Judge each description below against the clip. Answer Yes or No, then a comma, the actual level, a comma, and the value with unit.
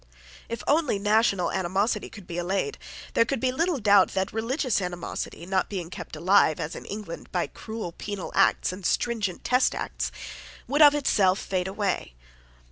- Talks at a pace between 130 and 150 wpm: No, average, 165 wpm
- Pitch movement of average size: Yes, average, 4.1 semitones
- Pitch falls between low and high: No, high, 200 Hz